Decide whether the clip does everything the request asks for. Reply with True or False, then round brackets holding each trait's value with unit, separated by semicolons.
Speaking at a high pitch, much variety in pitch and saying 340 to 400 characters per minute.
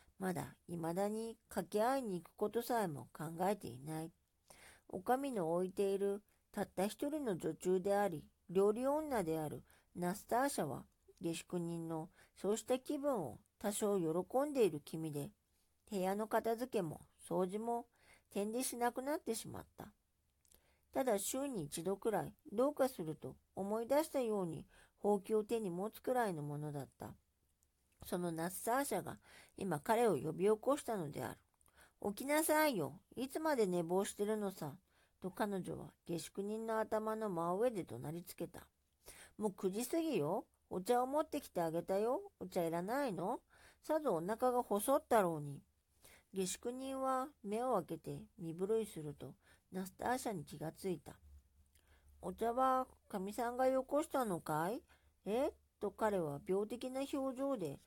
False (200 Hz; 6.6 semitones; 290 characters per minute)